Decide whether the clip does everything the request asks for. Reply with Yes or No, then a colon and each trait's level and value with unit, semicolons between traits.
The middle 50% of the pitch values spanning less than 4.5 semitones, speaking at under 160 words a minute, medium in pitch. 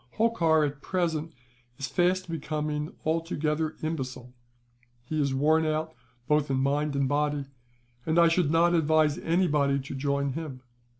Yes: narrow, 2.6 semitones; average, 140 wpm; medium, 150 Hz